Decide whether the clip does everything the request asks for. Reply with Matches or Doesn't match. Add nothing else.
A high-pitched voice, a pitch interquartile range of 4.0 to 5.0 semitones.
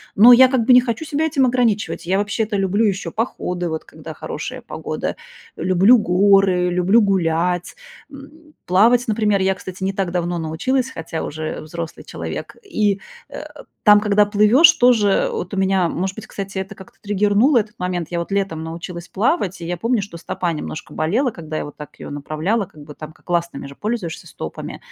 Matches